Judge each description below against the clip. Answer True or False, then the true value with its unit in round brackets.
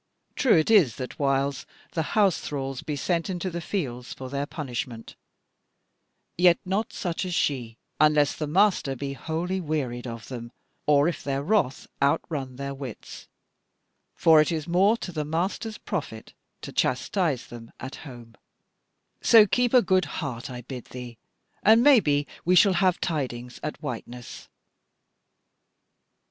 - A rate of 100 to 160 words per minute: True (150 wpm)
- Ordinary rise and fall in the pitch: False (5.8 semitones)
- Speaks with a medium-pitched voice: True (150 Hz)